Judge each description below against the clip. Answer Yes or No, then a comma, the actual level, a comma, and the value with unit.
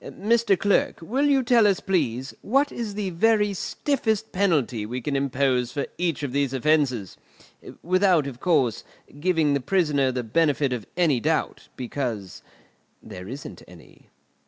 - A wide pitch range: Yes, wide, 7.6 semitones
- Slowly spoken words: No, average, 150 wpm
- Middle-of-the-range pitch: Yes, medium, 150 Hz